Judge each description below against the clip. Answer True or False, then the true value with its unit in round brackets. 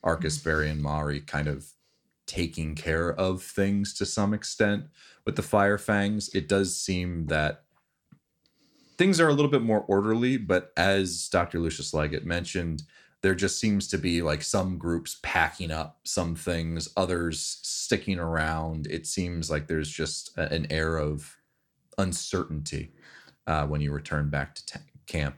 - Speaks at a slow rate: False (155 wpm)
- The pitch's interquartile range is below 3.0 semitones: False (4.2 semitones)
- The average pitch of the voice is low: True (85 Hz)